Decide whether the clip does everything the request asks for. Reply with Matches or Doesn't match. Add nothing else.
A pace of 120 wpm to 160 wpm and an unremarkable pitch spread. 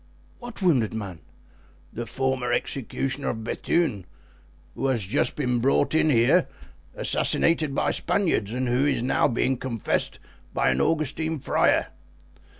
Matches